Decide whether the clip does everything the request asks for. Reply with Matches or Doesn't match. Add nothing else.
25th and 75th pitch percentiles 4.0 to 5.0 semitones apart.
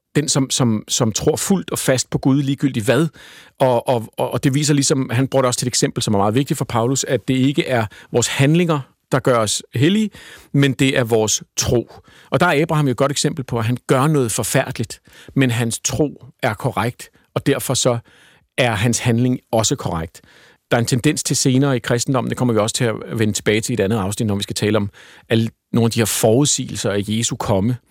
Doesn't match